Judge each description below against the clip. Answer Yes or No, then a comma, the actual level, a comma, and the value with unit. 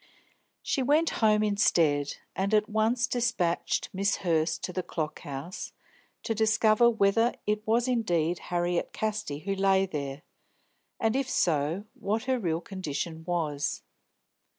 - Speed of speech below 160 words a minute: Yes, slow, 135 wpm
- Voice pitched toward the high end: Yes, high, 195 Hz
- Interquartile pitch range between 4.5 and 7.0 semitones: Yes, average, 4.9 semitones